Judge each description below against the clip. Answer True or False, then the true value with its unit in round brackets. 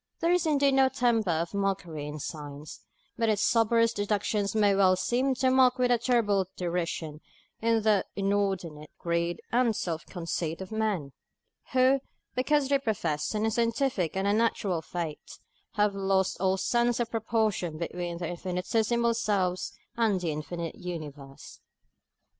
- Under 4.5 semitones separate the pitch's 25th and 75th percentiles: False (5.1 semitones)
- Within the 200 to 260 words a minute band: False (140 wpm)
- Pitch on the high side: True (200 Hz)